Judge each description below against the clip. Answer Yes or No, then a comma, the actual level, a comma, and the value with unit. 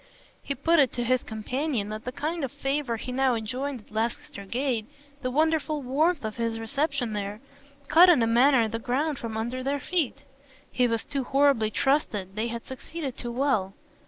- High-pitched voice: Yes, very high, 255 Hz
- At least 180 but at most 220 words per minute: Yes, average, 190 wpm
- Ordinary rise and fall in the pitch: Yes, average, 4.0 semitones